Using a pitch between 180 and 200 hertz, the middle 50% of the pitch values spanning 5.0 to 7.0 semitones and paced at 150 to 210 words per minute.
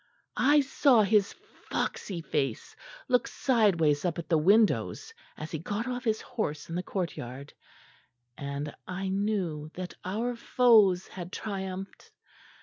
No: high, 190 Hz; wide, 5.5 semitones; slow, 135 wpm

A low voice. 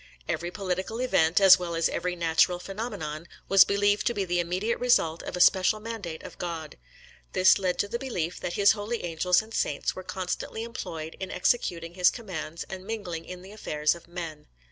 No: medium, 180 Hz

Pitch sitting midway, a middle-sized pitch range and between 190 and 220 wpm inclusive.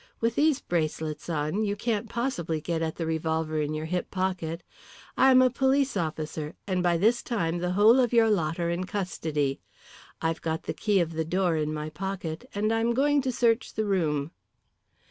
No: medium, 180 Hz; wide, 6.0 semitones; average, 195 wpm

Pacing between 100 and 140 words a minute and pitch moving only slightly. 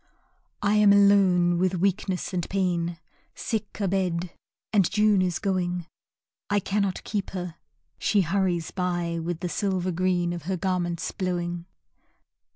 Yes: slow, 135 wpm; narrow, 2.2 semitones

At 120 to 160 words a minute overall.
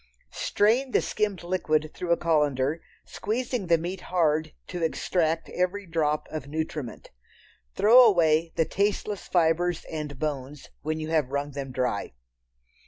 Yes: average, 140 wpm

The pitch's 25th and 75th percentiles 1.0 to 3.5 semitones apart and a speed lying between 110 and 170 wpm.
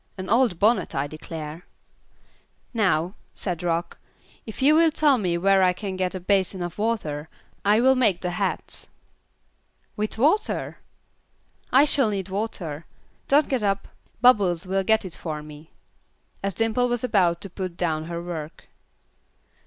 No: average, 4.8 semitones; average, 155 wpm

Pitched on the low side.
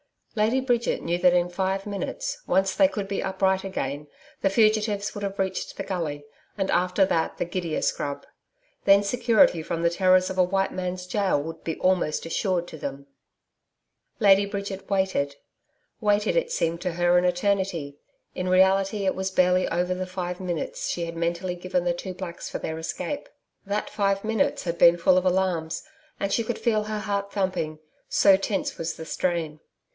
No: medium, 185 Hz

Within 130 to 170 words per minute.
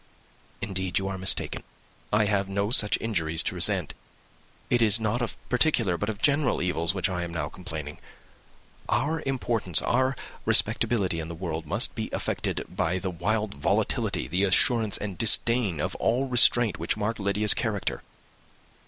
Yes: average, 160 wpm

